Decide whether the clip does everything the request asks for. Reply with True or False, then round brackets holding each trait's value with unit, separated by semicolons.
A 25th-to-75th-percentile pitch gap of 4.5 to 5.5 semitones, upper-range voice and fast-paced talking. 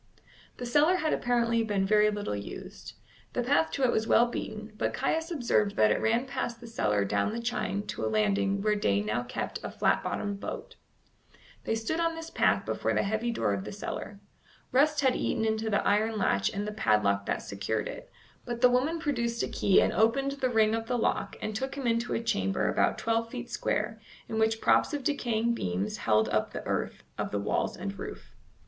False (3.6 semitones; 220 Hz; 210 wpm)